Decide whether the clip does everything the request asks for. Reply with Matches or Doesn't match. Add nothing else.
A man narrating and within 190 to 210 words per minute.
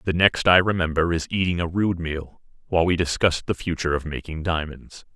Matches